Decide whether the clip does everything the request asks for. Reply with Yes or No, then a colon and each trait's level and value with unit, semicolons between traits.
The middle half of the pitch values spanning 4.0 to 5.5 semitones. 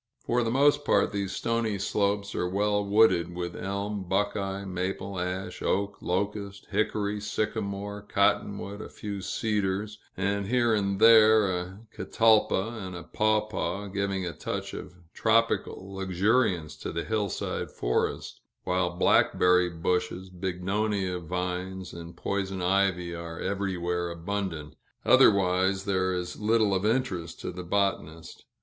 No: narrow, 2.4 semitones